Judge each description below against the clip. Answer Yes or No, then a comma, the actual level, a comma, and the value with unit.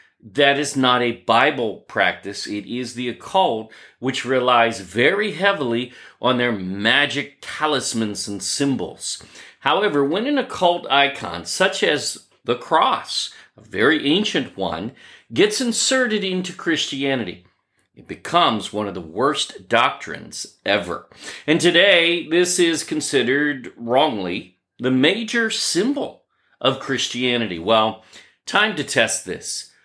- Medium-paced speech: No, slow, 125 wpm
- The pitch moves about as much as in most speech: No, wide, 6.9 semitones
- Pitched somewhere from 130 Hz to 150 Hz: Yes, low, 135 Hz